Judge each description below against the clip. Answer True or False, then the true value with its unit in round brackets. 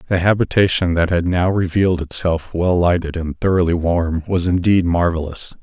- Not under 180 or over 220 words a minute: False (160 wpm)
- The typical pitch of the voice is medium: False (90 Hz)